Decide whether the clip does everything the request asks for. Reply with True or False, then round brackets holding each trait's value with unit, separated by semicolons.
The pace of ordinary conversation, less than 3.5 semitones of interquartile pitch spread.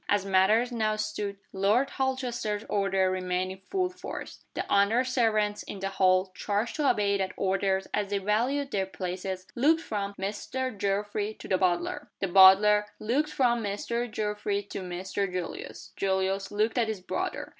True (165 wpm; 2.8 semitones)